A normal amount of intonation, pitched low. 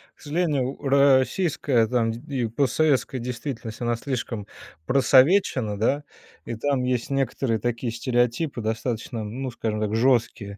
Yes: average, 3.2 semitones; low, 125 Hz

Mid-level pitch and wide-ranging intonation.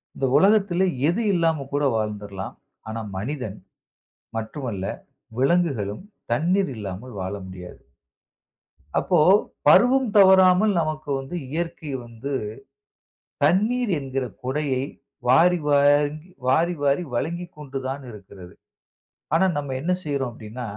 Yes: medium, 145 Hz; wide, 6.7 semitones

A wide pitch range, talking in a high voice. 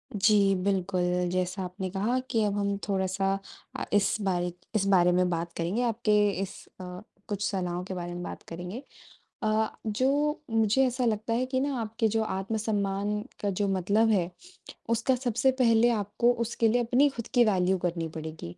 No: average, 3.5 semitones; high, 200 Hz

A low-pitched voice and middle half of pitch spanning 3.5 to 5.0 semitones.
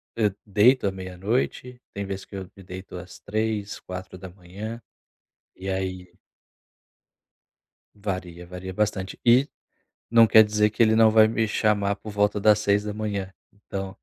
No: low, 100 Hz; narrow, 2.4 semitones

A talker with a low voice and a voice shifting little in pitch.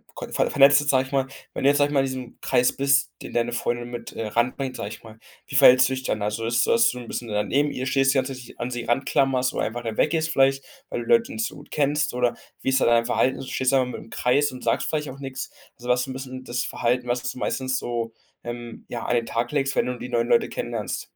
Yes: low, 125 Hz; narrow, 2.2 semitones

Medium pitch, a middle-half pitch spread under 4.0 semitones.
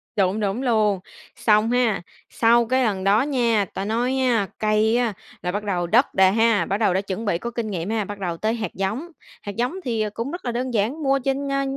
No: high, 220 Hz; average, 3.4 semitones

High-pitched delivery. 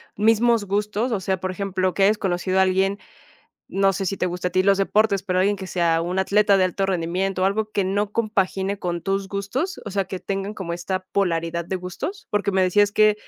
Yes: high, 195 Hz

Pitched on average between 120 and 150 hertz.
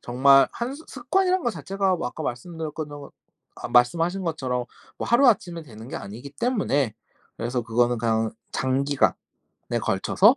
Yes: medium, 140 Hz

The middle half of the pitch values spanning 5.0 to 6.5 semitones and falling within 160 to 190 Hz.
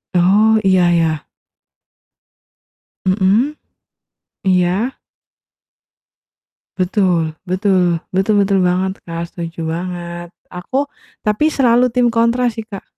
No: average, 4.0 semitones; medium, 185 Hz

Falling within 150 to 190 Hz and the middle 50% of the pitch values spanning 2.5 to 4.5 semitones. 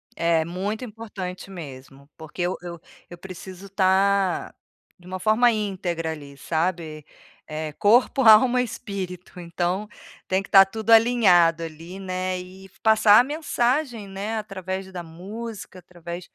Yes: medium, 185 Hz; average, 3.6 semitones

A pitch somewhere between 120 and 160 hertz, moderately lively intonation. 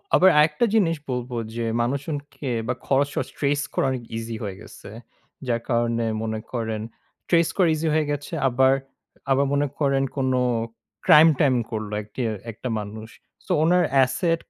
Yes: low, 135 Hz; average, 4.4 semitones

